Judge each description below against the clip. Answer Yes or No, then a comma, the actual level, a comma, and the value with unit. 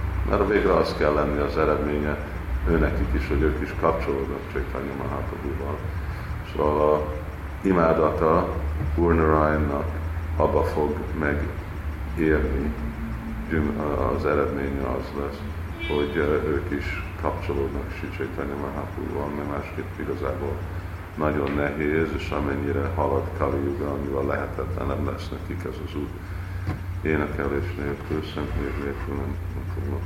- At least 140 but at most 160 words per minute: No, average, 115 wpm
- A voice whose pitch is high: No, very low, 80 Hz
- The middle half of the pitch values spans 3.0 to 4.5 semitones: Yes, average, 3.3 semitones